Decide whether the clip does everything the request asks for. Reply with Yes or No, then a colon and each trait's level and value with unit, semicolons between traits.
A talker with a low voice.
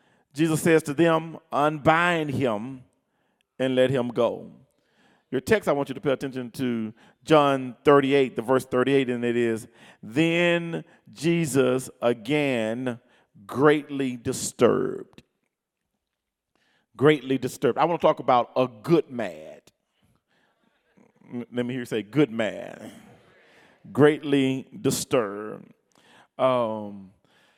Yes: low, 130 Hz